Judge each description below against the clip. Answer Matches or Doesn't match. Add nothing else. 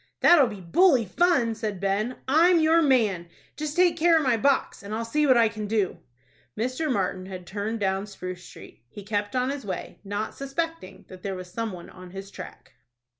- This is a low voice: Doesn't match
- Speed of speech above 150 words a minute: Matches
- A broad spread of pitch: Matches